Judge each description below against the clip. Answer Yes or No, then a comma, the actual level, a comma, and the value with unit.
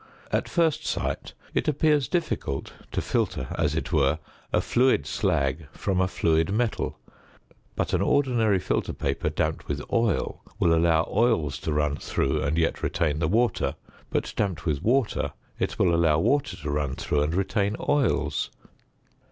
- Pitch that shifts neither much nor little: No, wide, 7.5 semitones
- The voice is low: Yes, very low, 85 Hz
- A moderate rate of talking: Yes, average, 160 wpm